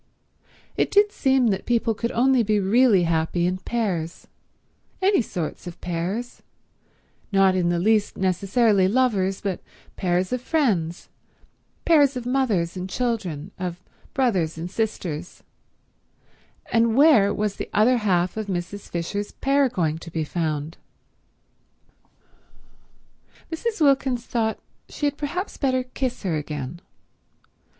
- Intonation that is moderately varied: No, wide, 6.2 semitones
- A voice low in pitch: No, high, 205 Hz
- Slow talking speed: Yes, slow, 125 wpm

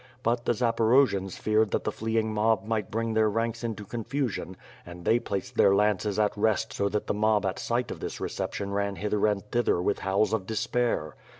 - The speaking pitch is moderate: No, low, 110 Hz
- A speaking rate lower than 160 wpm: No, fast, 205 wpm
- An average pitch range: No, narrow, 2.2 semitones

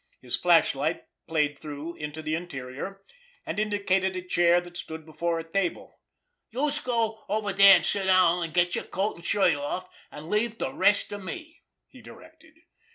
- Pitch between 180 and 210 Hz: Yes, medium, 185 Hz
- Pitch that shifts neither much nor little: Yes, average, 4.1 semitones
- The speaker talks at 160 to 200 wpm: Yes, average, 175 wpm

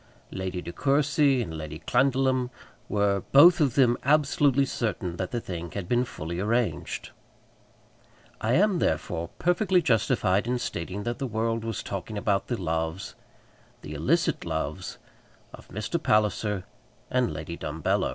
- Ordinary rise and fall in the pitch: No, wide, 6.3 semitones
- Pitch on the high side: No, low, 115 Hz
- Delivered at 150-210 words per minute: No, average, 140 wpm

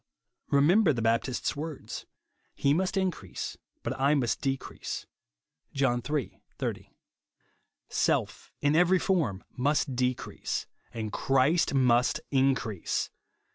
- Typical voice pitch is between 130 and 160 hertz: Yes, low, 135 Hz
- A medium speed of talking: No, slow, 105 wpm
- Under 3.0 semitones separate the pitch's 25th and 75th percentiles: No, average, 3.8 semitones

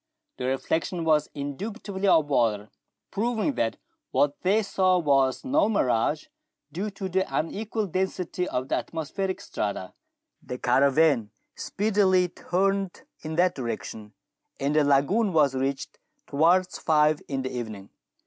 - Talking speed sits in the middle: No, slow, 130 wpm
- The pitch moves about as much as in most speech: No, wide, 6.1 semitones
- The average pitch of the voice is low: No, medium, 160 Hz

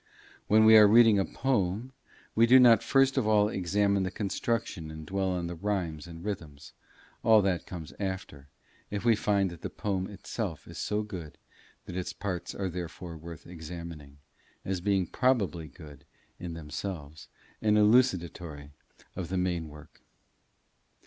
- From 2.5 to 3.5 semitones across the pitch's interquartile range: No, average, 4.0 semitones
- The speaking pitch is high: No, very low, 95 Hz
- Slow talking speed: No, average, 155 wpm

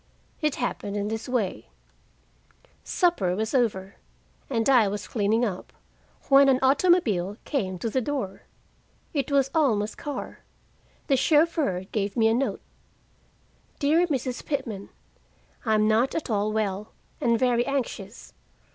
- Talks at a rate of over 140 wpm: No, slow, 135 wpm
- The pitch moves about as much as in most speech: Yes, average, 5.0 semitones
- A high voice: Yes, high, 235 Hz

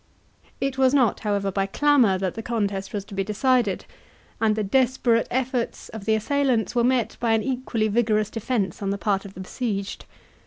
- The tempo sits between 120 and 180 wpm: No, average, 190 wpm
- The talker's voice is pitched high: Yes, high, 220 Hz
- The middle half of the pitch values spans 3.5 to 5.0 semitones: Yes, average, 4.0 semitones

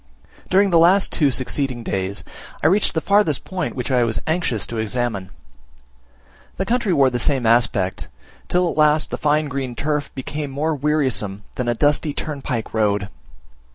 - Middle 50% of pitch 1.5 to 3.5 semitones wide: No, average, 4.8 semitones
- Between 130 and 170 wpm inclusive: Yes, average, 160 wpm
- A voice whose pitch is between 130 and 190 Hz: Yes, medium, 140 Hz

